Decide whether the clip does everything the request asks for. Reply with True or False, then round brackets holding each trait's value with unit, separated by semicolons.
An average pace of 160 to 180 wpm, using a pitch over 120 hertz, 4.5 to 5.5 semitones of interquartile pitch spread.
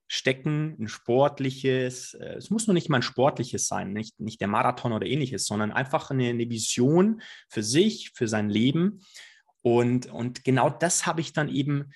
True (175 wpm; 130 Hz; 5.0 semitones)